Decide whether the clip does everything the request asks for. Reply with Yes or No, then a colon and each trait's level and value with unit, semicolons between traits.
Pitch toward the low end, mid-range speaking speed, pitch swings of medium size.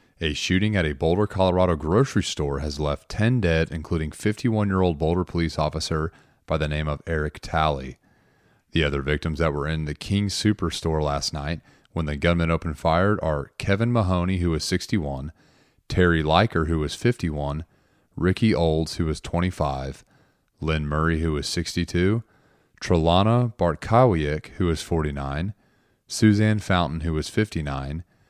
Yes: very low, 85 Hz; average, 150 wpm; average, 3.7 semitones